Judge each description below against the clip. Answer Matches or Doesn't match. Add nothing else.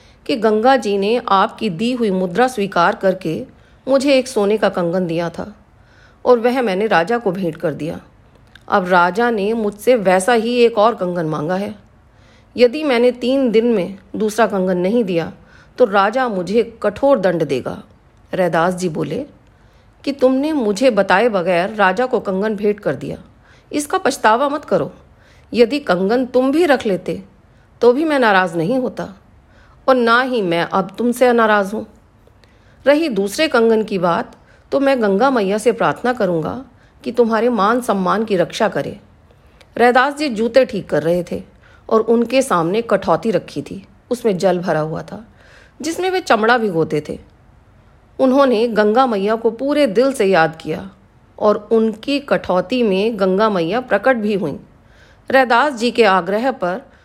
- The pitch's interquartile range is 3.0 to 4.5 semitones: Doesn't match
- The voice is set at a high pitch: Matches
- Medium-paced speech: Matches